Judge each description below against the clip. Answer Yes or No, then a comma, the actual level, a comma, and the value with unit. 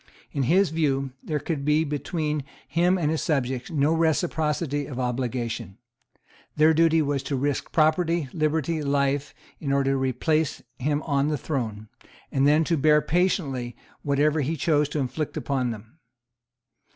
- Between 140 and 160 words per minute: Yes, average, 150 wpm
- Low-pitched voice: No, medium, 150 Hz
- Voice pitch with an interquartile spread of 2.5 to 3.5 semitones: Yes, average, 2.8 semitones